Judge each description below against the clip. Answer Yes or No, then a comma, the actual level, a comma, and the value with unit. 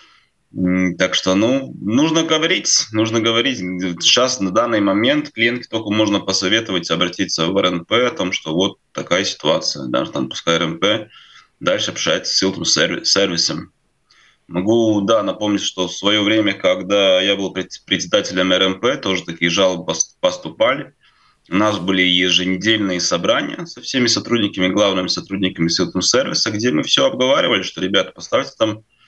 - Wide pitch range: No, average, 3.1 semitones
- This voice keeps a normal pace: Yes, average, 145 wpm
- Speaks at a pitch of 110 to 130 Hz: No, very low, 95 Hz